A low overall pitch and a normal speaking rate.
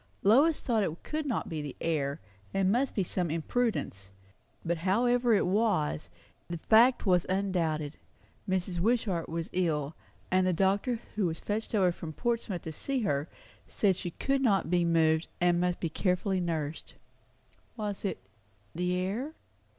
No: medium, 185 Hz; average, 160 wpm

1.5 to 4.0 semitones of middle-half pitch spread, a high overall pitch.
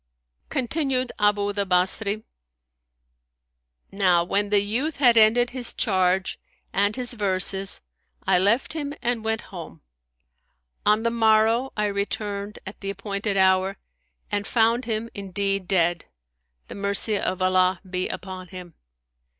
Yes: average, 2.9 semitones; high, 205 Hz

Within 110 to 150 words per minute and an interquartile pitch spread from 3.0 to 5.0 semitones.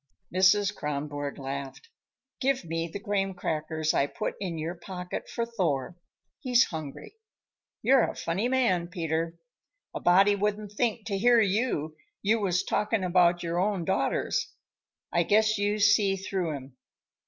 Yes: average, 145 wpm; average, 4.1 semitones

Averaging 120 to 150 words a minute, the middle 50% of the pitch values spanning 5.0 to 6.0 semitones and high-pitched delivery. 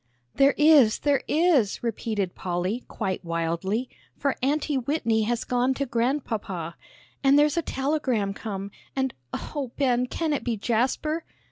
Yes: average, 140 wpm; average, 5.3 semitones; high, 245 Hz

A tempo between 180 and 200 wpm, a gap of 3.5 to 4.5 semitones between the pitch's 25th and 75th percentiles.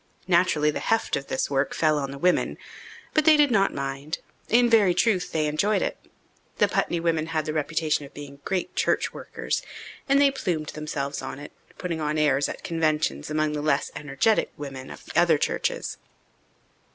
Yes: average, 185 wpm; average, 3.8 semitones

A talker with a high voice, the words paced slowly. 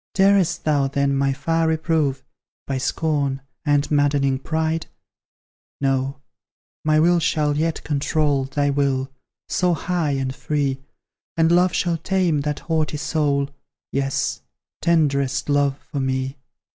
No: medium, 145 Hz; slow, 125 wpm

